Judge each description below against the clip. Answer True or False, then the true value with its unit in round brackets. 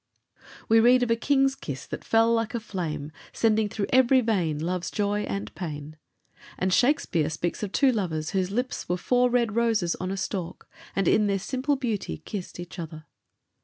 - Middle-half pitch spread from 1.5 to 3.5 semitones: False (5.3 semitones)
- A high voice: True (205 Hz)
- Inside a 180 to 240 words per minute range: True (185 wpm)